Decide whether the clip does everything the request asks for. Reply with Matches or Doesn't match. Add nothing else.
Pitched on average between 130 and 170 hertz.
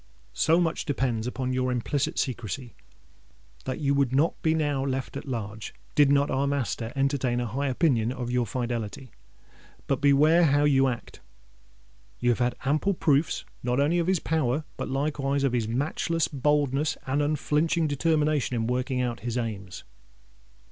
Matches